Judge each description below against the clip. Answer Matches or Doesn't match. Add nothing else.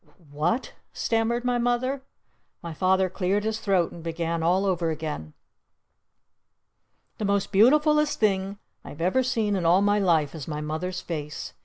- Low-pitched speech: Doesn't match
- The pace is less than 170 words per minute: Matches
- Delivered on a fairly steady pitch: Doesn't match